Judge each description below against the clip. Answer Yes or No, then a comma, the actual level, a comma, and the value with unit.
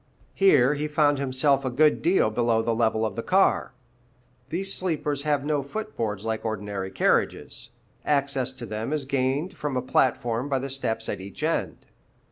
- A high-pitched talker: No, low, 135 Hz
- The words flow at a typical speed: Yes, average, 175 wpm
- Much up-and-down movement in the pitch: No, average, 4.5 semitones